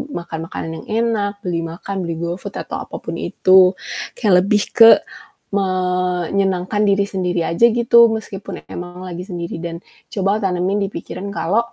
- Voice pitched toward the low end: No, medium, 185 Hz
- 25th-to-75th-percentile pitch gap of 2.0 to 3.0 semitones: Yes, narrow, 2.4 semitones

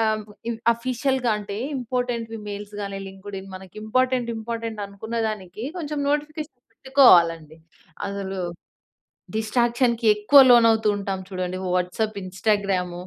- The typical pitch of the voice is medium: No, high, 220 Hz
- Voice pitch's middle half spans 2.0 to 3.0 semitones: No, average, 3.8 semitones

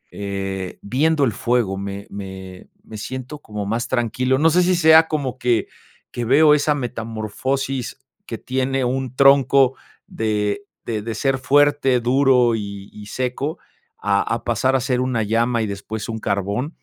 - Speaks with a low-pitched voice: Yes, low, 125 Hz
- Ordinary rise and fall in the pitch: Yes, average, 4.2 semitones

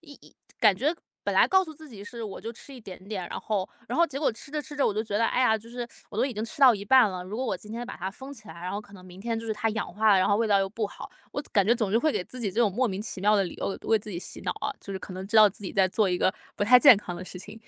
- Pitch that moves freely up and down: No, average, 3.5 semitones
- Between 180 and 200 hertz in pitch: No, high, 215 Hz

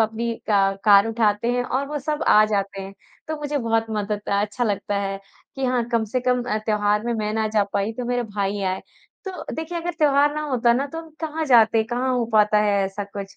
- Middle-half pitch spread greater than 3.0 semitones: Yes, average, 3.7 semitones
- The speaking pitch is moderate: No, high, 225 Hz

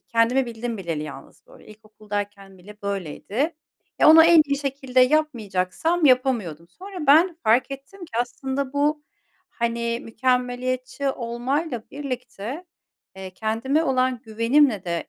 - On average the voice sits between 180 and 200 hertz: No, very high, 250 Hz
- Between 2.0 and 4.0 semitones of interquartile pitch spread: No, average, 4.7 semitones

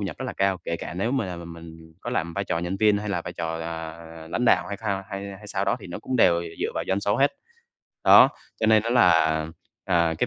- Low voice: Yes, very low, 95 Hz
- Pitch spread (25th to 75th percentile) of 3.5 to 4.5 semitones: Yes, average, 4.0 semitones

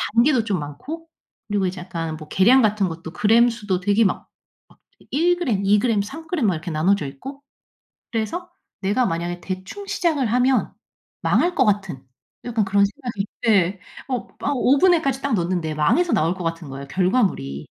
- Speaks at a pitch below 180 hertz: No, high, 205 Hz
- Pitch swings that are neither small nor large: No, wide, 6.5 semitones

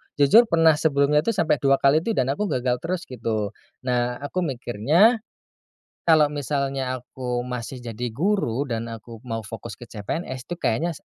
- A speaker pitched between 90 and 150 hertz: Yes, low, 135 Hz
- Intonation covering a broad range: No, average, 4.7 semitones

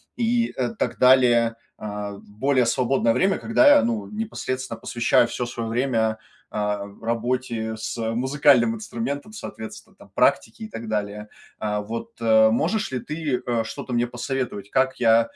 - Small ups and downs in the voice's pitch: No, average, 3.3 semitones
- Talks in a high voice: No, low, 120 Hz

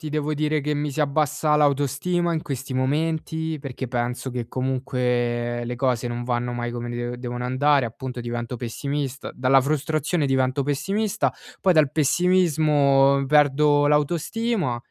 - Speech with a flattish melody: No, average, 3.6 semitones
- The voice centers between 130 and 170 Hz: Yes, medium, 140 Hz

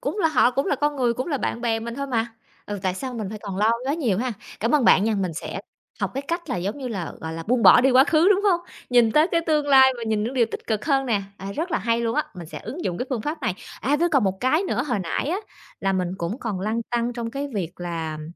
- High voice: Yes, high, 240 Hz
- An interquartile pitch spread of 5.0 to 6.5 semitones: Yes, average, 5.3 semitones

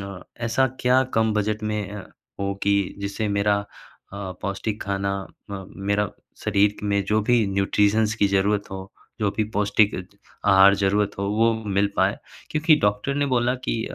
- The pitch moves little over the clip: Yes, narrow, 1.7 semitones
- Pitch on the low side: Yes, low, 105 Hz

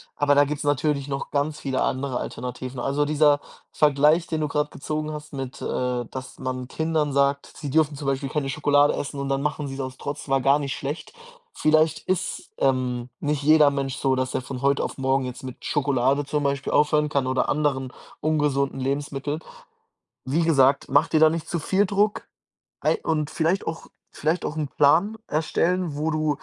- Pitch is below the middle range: No, medium, 145 Hz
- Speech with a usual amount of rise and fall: No, narrow, 2.2 semitones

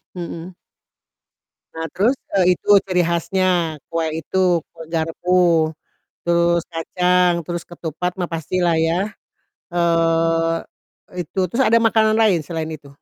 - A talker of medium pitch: Yes, medium, 170 Hz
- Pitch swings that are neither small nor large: No, narrow, 1.7 semitones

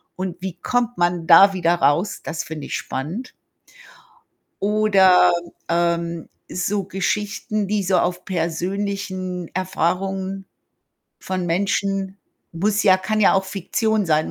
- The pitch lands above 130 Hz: Yes, high, 190 Hz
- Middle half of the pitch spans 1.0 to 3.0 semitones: Yes, narrow, 2.5 semitones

